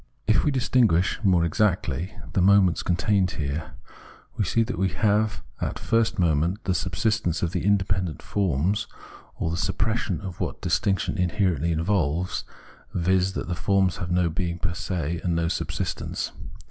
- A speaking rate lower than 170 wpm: Yes, average, 160 wpm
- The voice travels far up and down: No, average, 3.2 semitones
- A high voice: No, very low, 90 Hz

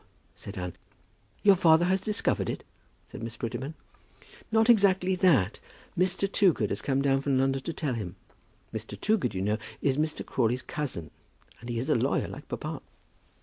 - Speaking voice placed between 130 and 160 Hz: Yes, low, 135 Hz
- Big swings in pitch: Yes, wide, 7.9 semitones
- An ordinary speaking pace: Yes, average, 170 wpm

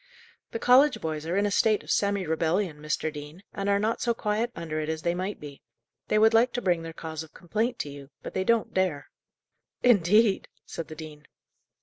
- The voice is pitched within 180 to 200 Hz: Yes, medium, 185 Hz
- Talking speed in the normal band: No, fast, 215 wpm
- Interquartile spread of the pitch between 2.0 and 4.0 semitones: No, average, 5.2 semitones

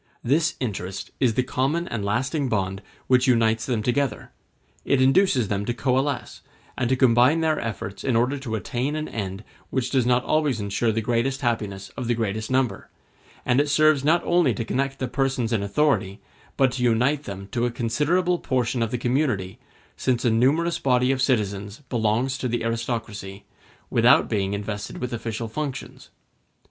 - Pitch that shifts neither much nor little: Yes, average, 3.5 semitones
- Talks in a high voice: No, low, 120 Hz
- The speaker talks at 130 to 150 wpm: No, average, 175 wpm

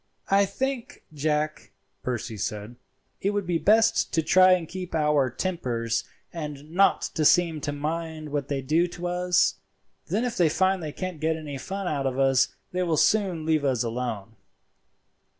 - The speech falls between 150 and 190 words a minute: Yes, average, 170 wpm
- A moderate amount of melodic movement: Yes, average, 4.8 semitones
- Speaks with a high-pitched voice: No, medium, 160 Hz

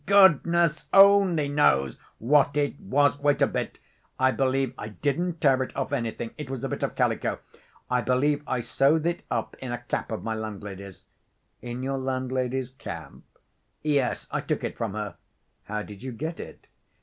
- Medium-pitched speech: No, low, 130 Hz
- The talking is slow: No, average, 175 wpm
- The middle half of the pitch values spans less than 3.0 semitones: No, average, 3.9 semitones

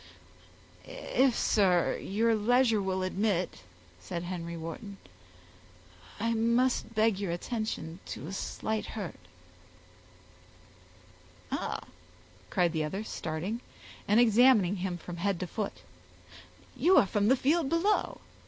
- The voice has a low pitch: No, high, 205 Hz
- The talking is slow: Yes, slow, 115 wpm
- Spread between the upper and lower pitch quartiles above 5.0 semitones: No, average, 4.6 semitones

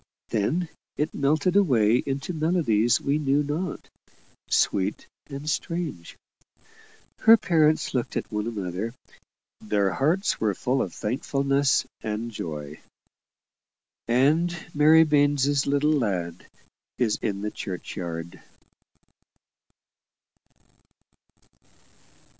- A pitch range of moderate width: No, wide, 6.3 semitones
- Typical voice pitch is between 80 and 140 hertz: Yes, low, 135 Hz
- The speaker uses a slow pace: Yes, slow, 95 wpm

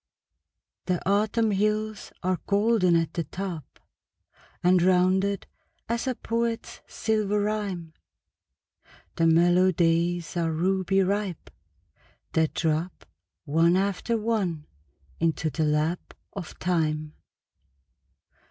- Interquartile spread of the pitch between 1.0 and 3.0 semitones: No, average, 3.7 semitones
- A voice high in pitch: No, medium, 180 Hz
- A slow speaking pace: Yes, slow, 100 wpm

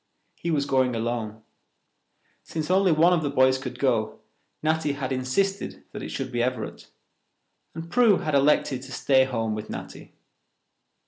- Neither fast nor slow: Yes, average, 155 wpm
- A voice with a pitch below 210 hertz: Yes, low, 135 Hz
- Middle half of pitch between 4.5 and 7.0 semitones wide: No, average, 3.9 semitones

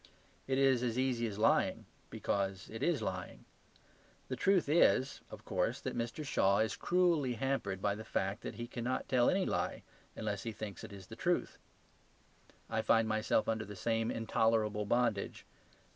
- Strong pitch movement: No, average, 3.6 semitones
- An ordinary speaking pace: Yes, average, 170 wpm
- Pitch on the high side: No, low, 115 Hz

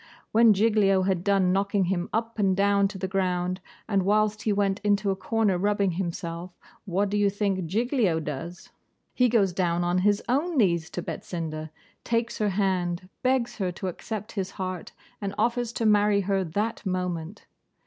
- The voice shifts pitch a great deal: No, narrow, 2.5 semitones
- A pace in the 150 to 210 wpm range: Yes, average, 175 wpm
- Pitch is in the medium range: No, high, 195 Hz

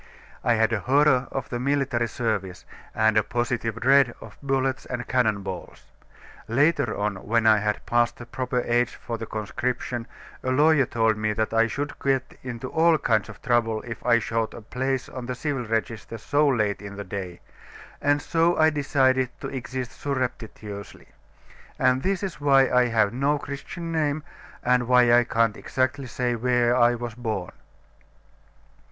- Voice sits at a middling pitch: No, low, 120 Hz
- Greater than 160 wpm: Yes, average, 170 wpm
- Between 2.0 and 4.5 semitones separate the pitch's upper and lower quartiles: Yes, average, 3.0 semitones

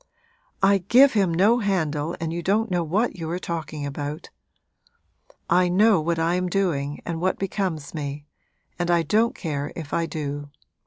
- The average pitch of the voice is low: No, medium, 170 Hz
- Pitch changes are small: No, average, 4.1 semitones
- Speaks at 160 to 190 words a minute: Yes, average, 170 wpm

